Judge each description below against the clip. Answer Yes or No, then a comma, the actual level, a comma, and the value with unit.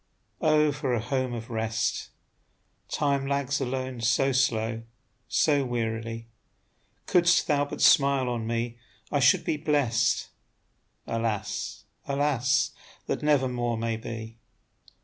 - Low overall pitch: Yes, low, 125 Hz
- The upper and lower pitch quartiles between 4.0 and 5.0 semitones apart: No, average, 3.6 semitones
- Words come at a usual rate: No, slow, 120 wpm